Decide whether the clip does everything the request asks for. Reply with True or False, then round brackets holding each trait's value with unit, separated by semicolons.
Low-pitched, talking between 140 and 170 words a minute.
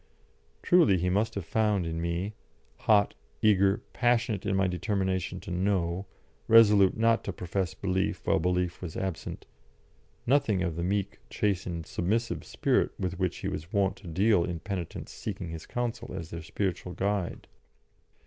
True (95 Hz; 155 wpm)